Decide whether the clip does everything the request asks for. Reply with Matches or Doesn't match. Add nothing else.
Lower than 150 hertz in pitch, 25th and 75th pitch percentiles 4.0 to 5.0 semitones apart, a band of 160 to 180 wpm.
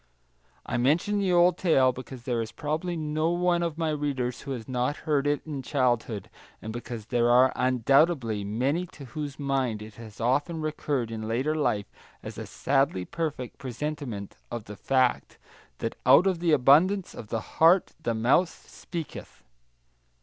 Matches